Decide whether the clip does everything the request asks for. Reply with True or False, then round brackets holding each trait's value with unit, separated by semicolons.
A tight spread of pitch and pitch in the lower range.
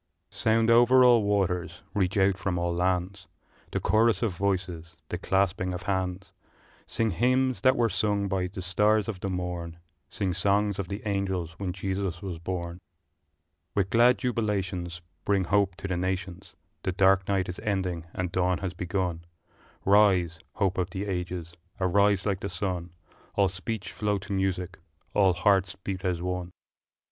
True (2.2 semitones; 95 Hz)